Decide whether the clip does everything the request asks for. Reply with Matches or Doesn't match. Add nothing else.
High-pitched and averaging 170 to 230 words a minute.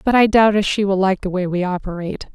Doesn't match